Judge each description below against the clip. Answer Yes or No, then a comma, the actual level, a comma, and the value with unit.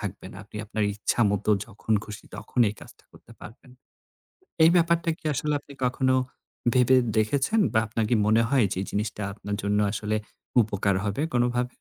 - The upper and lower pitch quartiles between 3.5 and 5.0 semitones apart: Yes, average, 3.8 semitones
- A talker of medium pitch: No, low, 110 Hz